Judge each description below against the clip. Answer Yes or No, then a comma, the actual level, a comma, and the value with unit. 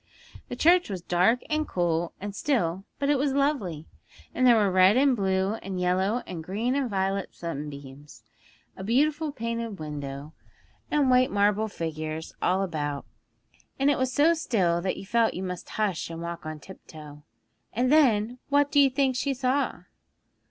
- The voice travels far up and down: Yes, wide, 7.3 semitones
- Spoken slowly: No, average, 170 wpm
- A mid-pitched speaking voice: No, high, 200 Hz